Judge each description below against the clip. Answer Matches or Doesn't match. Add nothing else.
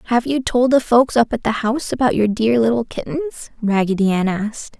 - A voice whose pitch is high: Matches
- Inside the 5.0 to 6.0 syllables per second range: Matches